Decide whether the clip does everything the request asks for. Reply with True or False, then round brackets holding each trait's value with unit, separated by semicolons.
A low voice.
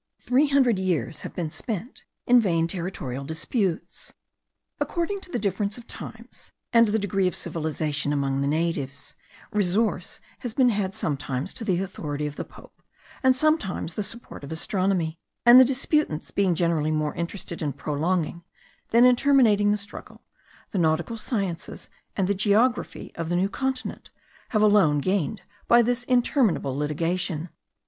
False (190 Hz)